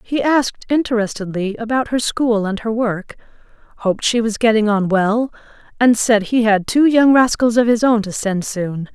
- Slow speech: No, average, 190 wpm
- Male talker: No, female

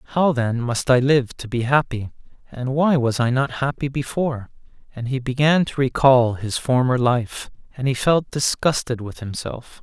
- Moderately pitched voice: No, low, 130 Hz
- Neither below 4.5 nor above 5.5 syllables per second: Yes, 4.6 syllables/s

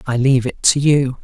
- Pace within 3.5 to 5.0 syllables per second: No, 5.5 syllables/s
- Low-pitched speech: Yes, low, 130 Hz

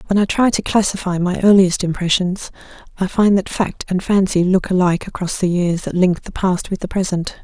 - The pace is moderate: No, fast, 210 wpm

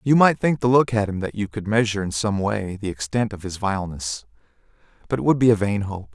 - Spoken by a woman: No, male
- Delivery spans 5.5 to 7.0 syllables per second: Yes, 6.0 syllables/s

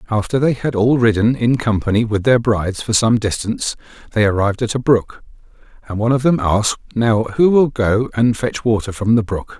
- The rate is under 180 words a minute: No, fast, 205 wpm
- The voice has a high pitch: No, low, 115 Hz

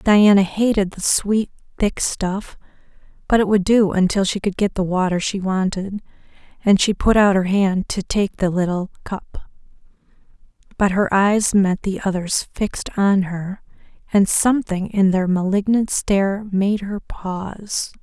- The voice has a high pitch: Yes, high, 195 Hz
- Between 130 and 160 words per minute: Yes, average, 155 wpm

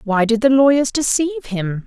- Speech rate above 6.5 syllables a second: No, 5.6 syllables/s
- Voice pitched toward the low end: No, high, 245 Hz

